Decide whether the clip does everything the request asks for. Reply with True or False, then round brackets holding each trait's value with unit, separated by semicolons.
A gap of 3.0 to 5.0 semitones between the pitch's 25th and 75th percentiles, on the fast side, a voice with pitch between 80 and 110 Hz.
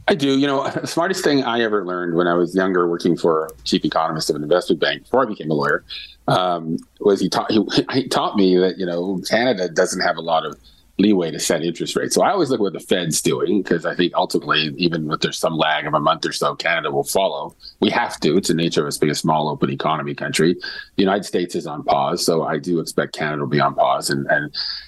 True (3.7 semitones; 255 wpm; 85 Hz)